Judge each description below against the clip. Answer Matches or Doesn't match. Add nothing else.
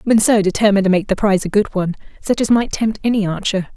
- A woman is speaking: Matches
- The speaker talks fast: Matches